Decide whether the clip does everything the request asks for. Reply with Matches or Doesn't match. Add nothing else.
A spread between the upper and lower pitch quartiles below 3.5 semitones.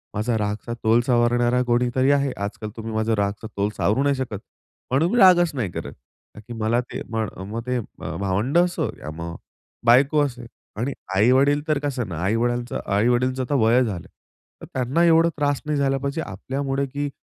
Doesn't match